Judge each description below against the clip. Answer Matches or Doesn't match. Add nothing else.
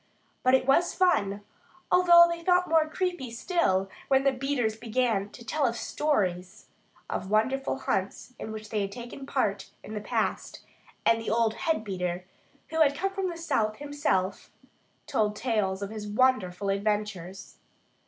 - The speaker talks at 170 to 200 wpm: Doesn't match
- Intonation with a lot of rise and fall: Matches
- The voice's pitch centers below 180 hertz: Doesn't match